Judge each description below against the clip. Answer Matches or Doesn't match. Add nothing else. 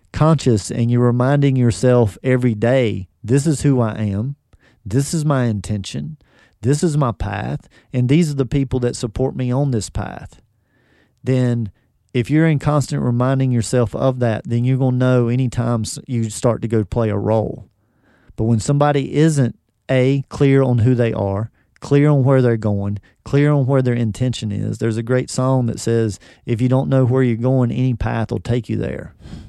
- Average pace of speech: Matches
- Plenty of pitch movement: Doesn't match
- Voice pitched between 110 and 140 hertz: Matches